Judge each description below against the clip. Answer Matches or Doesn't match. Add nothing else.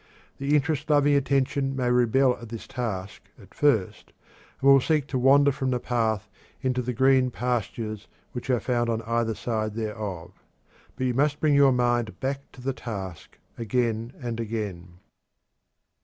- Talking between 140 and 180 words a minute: Matches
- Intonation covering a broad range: Doesn't match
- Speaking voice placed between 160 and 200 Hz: Doesn't match